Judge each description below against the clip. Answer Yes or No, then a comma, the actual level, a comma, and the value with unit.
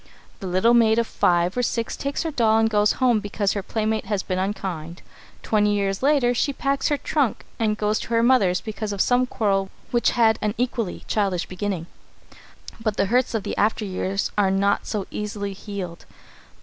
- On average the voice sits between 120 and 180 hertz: No, high, 210 Hz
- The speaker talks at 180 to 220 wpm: Yes, average, 190 wpm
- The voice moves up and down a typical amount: Yes, average, 3.1 semitones